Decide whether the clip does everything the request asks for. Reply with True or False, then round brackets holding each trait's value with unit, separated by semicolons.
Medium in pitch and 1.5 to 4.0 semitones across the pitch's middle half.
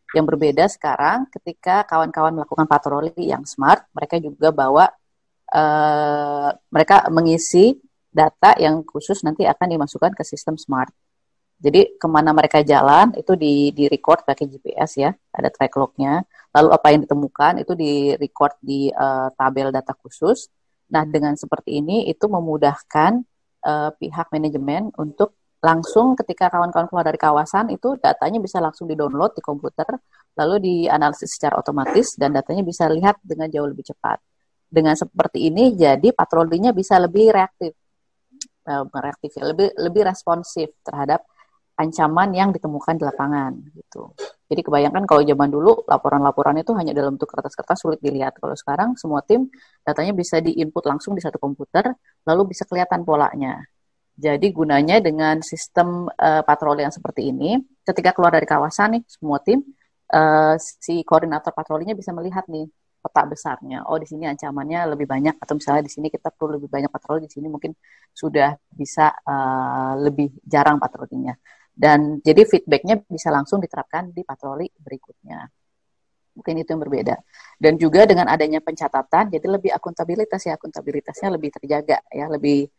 True (155 Hz; 3.5 semitones)